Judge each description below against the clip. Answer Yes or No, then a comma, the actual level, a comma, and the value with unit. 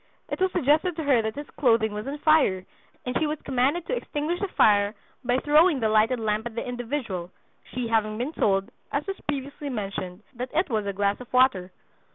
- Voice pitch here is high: Yes, very high, 250 Hz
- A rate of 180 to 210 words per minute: Yes, fast, 205 wpm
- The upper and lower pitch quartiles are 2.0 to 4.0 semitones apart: No, wide, 5.5 semitones